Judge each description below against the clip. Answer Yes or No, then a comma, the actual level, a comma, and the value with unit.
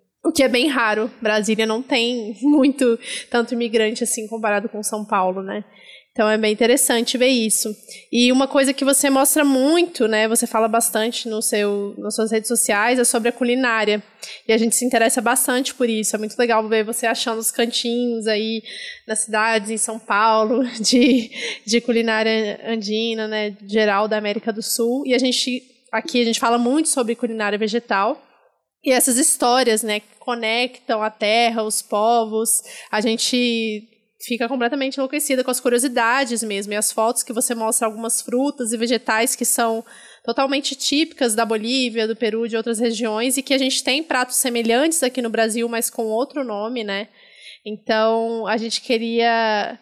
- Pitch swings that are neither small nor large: No, narrow, 2.2 semitones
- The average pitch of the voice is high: Yes, high, 230 Hz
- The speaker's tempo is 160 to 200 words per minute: Yes, average, 175 wpm